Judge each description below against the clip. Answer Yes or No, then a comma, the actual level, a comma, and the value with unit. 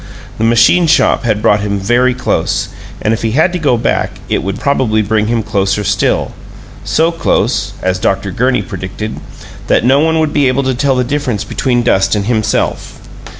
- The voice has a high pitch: No, low, 120 Hz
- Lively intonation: No, average, 4.3 semitones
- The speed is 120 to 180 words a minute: No, average, 190 wpm